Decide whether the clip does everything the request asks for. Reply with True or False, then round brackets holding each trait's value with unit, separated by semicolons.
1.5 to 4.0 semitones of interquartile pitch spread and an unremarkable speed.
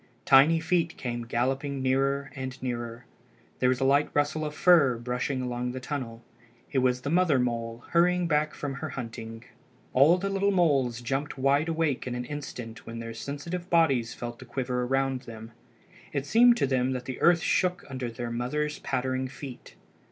True (3.5 semitones; 180 wpm)